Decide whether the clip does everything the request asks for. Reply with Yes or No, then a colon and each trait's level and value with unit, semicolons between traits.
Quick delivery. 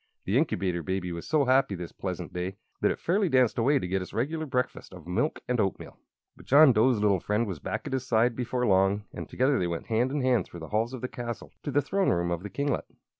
Yes: fast, 250 wpm